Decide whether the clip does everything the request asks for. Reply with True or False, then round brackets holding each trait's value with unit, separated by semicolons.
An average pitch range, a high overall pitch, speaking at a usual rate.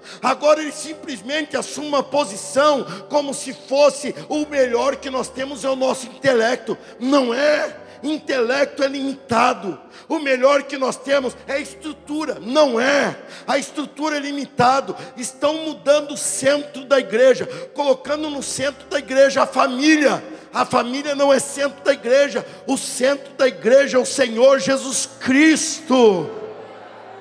False (1.9 semitones; 275 Hz; 145 wpm)